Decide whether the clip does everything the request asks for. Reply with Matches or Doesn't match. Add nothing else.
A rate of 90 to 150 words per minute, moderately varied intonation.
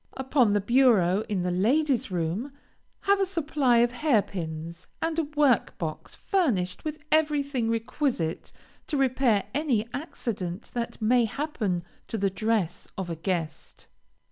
Doesn't match